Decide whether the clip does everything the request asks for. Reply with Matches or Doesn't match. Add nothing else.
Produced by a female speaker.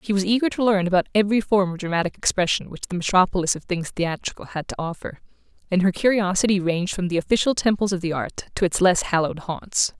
Matches